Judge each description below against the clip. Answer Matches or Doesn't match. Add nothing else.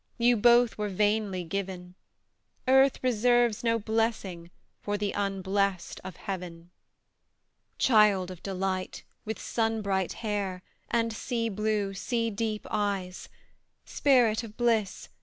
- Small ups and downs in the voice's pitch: Doesn't match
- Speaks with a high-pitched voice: Matches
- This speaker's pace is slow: Matches